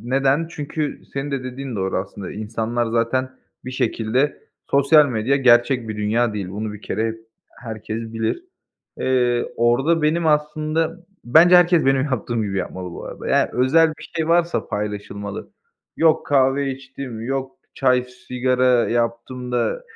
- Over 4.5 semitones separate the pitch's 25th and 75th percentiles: No, average, 3.8 semitones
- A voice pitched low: Yes, low, 125 Hz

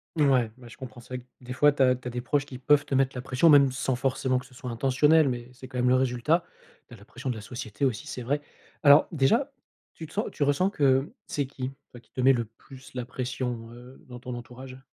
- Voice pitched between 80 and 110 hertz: No, low, 130 Hz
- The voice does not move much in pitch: Yes, narrow, 2.1 semitones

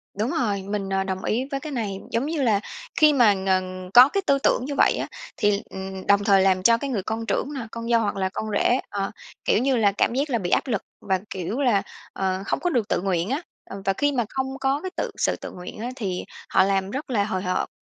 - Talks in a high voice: Yes, high, 210 Hz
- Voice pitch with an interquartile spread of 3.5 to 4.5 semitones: No, average, 5.1 semitones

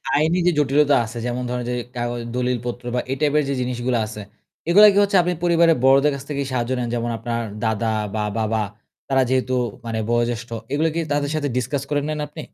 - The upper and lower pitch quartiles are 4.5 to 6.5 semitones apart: No, average, 3.7 semitones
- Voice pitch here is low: Yes, low, 130 Hz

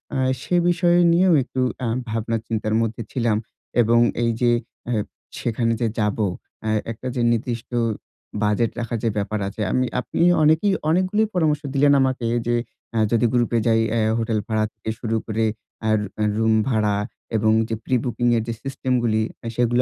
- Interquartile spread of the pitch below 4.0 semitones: Yes, average, 2.7 semitones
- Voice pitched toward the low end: Yes, low, 115 Hz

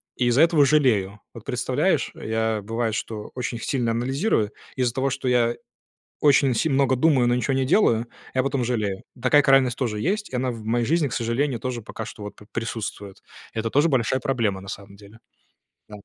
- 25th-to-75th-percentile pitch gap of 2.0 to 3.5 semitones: Yes, average, 3.2 semitones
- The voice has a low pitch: Yes, low, 120 Hz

